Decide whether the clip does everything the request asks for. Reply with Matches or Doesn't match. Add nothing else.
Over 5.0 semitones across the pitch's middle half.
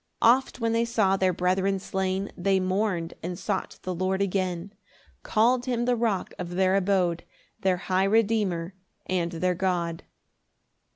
Doesn't match